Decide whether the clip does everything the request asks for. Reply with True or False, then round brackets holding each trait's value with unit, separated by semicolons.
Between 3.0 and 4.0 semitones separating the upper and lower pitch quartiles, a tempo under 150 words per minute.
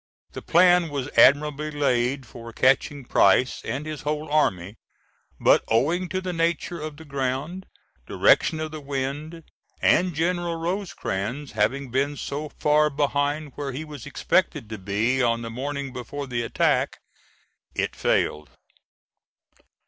True (3.4 semitones; 140 wpm)